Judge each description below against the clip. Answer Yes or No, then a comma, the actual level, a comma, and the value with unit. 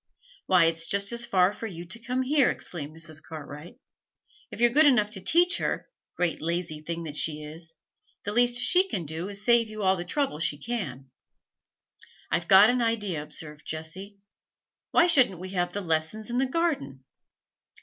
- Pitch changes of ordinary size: No, wide, 6.7 semitones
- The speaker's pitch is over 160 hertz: Yes, high, 190 Hz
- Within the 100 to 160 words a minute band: No, average, 180 wpm